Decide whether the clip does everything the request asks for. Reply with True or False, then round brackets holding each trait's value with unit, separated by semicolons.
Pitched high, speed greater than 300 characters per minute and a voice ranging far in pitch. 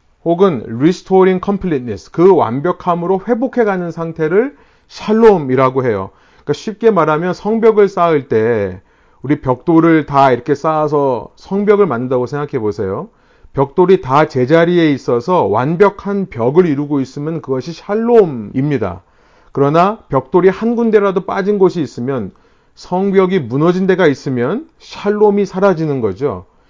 False (170 Hz; 340 characters per minute; 5.9 semitones)